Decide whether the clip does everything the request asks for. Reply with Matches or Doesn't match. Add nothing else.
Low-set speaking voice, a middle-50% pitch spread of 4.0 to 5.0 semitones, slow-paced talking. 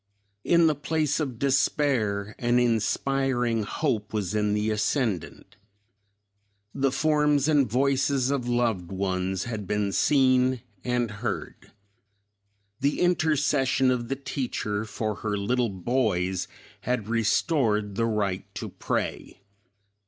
Matches